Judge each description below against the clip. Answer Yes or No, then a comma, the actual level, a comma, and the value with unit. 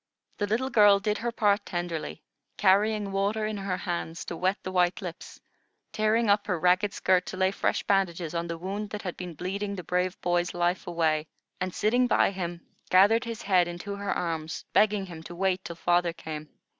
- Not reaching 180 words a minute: No, average, 195 wpm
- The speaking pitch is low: No, medium, 185 Hz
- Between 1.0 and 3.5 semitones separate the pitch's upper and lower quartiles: Yes, average, 2.8 semitones